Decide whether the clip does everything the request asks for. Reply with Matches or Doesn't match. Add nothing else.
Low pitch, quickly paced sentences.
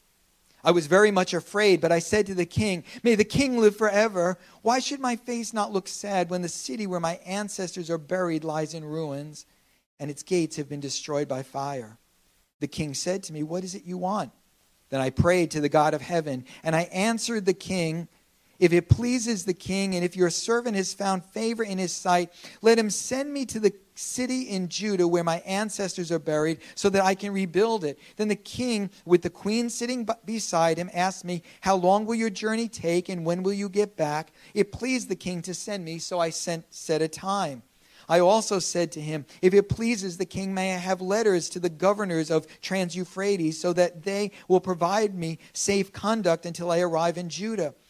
Doesn't match